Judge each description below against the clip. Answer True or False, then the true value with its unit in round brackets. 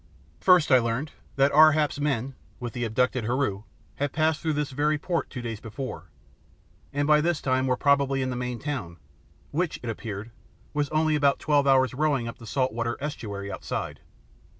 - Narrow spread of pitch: False (3.8 semitones)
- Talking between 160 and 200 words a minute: True (185 wpm)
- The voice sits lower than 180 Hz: True (135 Hz)